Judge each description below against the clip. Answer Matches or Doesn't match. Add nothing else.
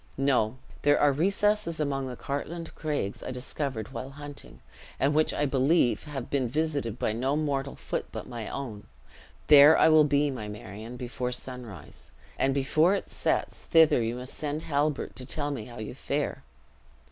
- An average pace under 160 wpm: Doesn't match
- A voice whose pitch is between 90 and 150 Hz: Matches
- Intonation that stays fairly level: Doesn't match